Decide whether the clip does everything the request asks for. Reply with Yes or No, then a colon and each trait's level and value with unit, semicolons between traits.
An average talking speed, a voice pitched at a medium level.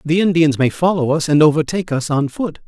No: fast, 225 wpm; medium, 160 Hz